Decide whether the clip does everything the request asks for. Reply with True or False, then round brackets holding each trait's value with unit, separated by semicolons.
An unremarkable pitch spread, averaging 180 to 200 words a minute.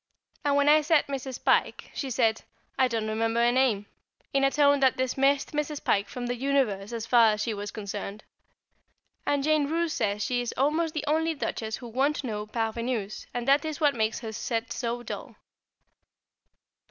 True (4.2 semitones; 185 wpm)